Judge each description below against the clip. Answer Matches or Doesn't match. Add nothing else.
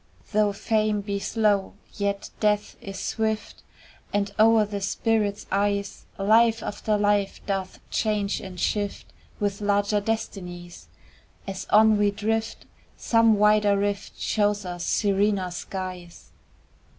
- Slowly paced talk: Matches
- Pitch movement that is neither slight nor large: Doesn't match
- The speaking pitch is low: Doesn't match